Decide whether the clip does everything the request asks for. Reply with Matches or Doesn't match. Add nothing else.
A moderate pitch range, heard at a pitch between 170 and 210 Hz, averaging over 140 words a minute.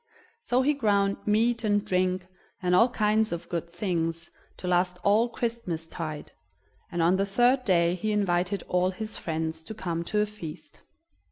Matches